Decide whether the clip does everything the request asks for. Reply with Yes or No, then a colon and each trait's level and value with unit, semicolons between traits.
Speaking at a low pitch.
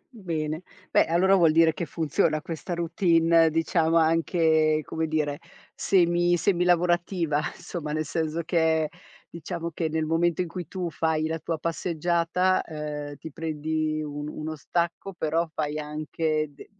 No: medium, 160 Hz